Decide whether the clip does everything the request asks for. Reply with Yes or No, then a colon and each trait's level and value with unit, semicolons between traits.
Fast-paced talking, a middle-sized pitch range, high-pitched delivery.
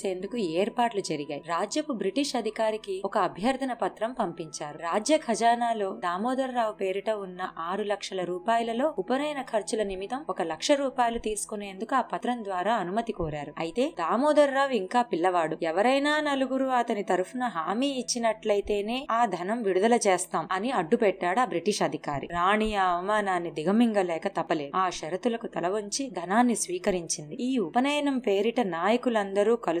Yes: fast, 135 wpm; average, 4.8 semitones; high, 210 Hz